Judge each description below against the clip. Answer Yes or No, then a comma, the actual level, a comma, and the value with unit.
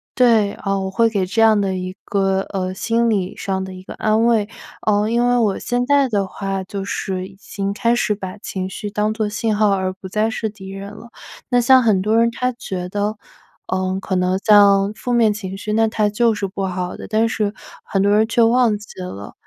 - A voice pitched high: Yes, high, 205 Hz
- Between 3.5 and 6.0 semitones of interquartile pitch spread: No, average, 2.7 semitones